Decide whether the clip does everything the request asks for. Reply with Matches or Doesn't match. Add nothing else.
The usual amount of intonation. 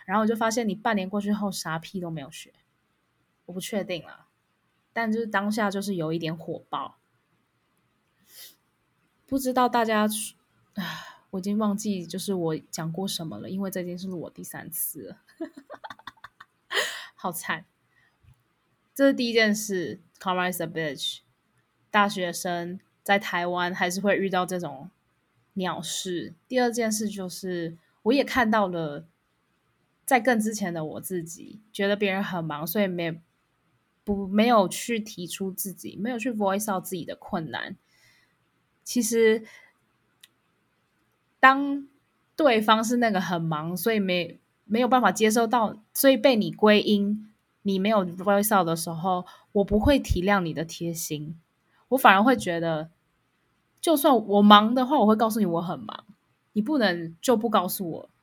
Matches